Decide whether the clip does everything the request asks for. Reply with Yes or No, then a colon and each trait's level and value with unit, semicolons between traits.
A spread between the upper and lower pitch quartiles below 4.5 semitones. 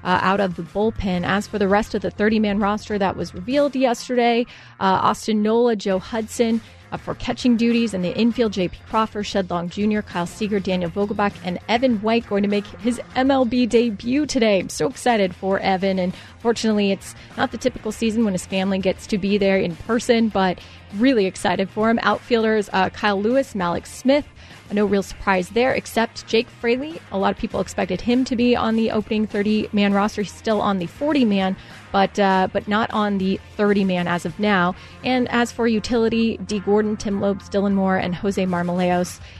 Yes: average, 3.2 semitones